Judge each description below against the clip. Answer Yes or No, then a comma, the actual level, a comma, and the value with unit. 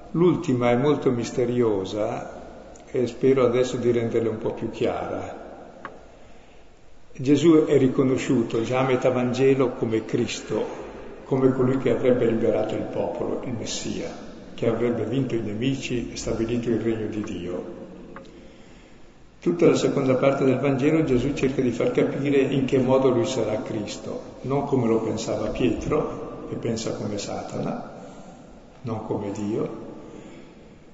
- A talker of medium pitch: No, low, 125 Hz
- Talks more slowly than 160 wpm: Yes, average, 140 wpm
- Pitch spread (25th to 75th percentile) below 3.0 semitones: Yes, narrow, 2.6 semitones